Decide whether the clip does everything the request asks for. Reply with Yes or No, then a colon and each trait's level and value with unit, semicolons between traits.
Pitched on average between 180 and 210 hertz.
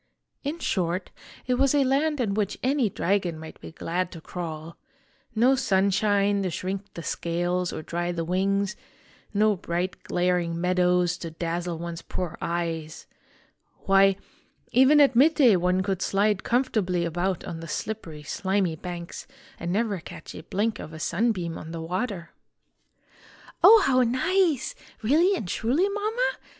Yes: high, 190 Hz